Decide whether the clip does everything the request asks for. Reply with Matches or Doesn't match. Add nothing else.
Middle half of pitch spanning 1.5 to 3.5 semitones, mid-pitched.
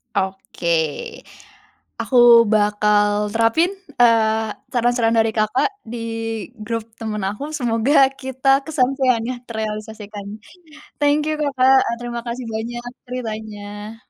Doesn't match